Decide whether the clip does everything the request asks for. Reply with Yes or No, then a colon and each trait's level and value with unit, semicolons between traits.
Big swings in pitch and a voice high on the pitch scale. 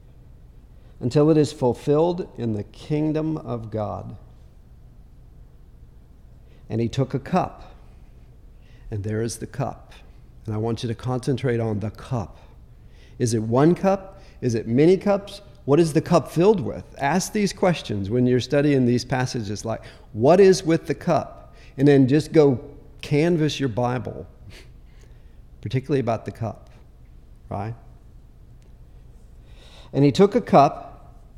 No: wide, 6.1 semitones; low, 125 Hz